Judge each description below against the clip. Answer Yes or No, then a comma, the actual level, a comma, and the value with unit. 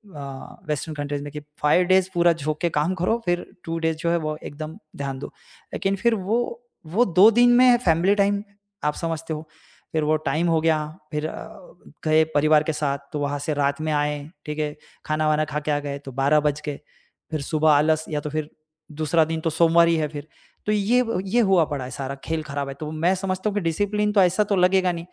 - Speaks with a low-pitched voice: No, medium, 155 Hz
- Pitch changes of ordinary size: Yes, average, 3.3 semitones